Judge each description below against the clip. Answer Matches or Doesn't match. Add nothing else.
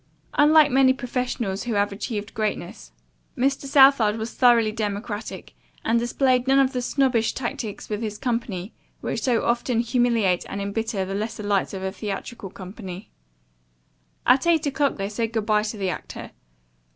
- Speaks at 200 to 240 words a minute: Doesn't match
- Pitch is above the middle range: Matches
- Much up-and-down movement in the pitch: Doesn't match